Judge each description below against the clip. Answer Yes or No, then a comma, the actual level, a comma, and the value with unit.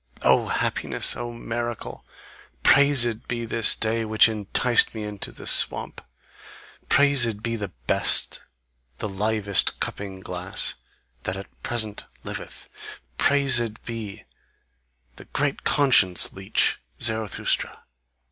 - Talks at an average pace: No, slow, 110 wpm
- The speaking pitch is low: Yes, low, 110 Hz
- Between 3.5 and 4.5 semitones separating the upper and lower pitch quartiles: No, average, 2.7 semitones